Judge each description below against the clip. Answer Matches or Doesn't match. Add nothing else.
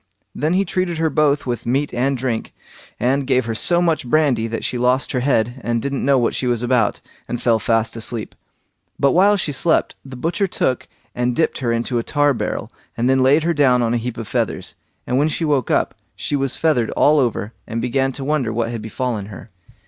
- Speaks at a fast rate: Matches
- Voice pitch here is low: Matches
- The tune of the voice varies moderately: Matches